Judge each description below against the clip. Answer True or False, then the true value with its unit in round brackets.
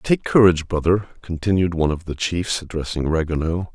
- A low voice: True (85 Hz)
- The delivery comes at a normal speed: True (160 wpm)